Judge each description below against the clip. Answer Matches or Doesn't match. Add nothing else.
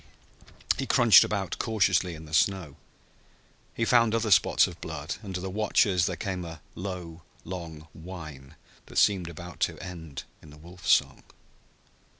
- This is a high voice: Doesn't match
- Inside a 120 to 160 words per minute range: Matches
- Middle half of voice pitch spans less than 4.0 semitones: Matches